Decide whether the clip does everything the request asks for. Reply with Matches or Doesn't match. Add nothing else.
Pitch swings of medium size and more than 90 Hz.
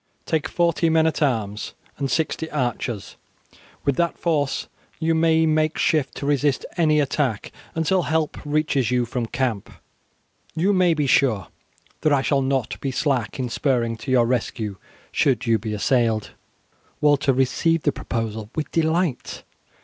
Matches